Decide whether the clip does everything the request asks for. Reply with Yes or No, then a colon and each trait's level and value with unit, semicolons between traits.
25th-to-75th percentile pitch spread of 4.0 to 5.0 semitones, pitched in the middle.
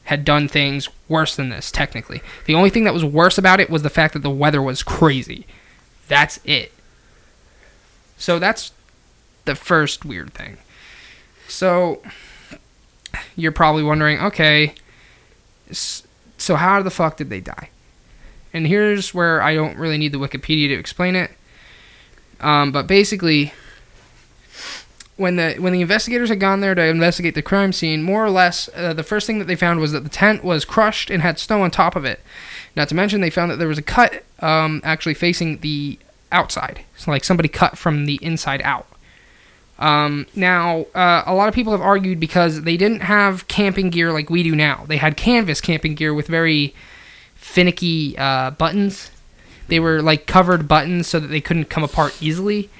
No: average, 3.4 semitones; medium, 165 Hz